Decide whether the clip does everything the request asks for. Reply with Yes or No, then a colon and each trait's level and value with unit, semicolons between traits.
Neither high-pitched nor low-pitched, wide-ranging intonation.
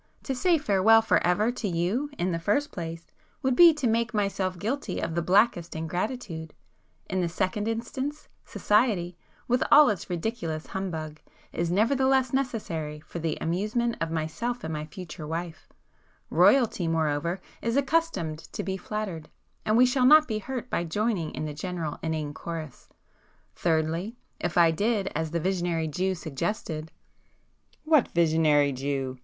Yes: medium, 180 Hz; wide, 6.2 semitones